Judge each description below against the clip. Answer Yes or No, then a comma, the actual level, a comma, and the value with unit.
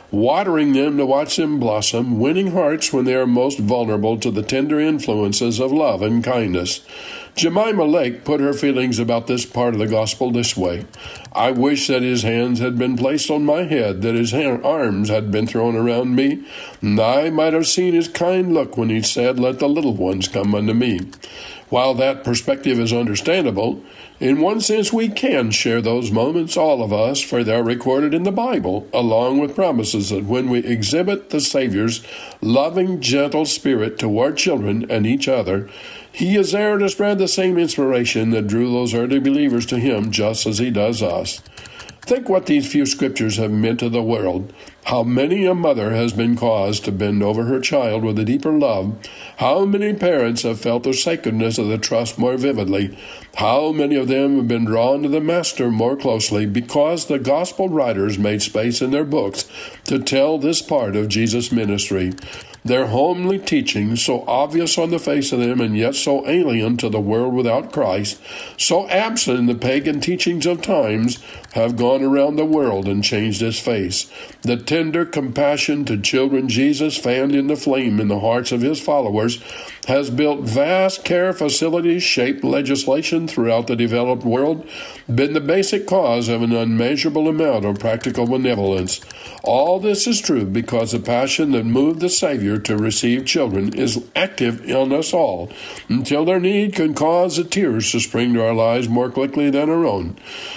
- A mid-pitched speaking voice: No, low, 125 Hz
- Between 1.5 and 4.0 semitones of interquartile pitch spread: No, average, 5.1 semitones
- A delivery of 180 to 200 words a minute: Yes, average, 185 wpm